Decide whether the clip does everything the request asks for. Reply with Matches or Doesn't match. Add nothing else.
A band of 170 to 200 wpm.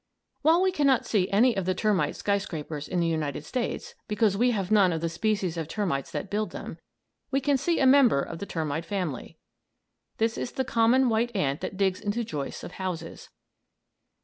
Matches